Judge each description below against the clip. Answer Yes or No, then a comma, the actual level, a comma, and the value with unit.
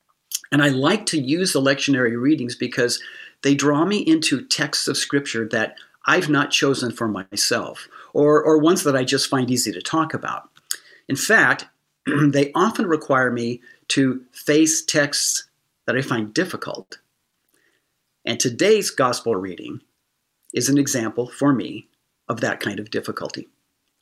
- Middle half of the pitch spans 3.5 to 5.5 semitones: Yes, average, 4.0 semitones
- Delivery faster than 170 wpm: No, average, 150 wpm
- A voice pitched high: No, medium, 140 Hz